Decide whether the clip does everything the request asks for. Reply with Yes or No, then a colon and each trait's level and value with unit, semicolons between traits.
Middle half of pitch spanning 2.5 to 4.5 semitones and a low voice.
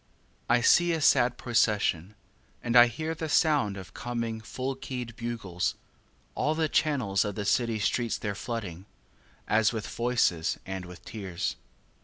Yes: average, 3.8 semitones; low, 115 Hz